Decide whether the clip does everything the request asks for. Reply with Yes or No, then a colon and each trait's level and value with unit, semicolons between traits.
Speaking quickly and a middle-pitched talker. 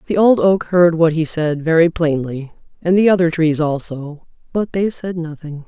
No: average, 190 wpm; medium, 165 Hz